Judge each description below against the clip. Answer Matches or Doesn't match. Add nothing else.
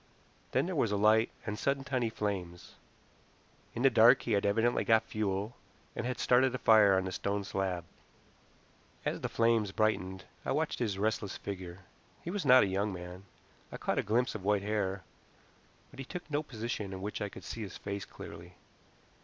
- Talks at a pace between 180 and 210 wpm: Matches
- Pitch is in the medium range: Doesn't match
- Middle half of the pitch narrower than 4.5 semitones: Matches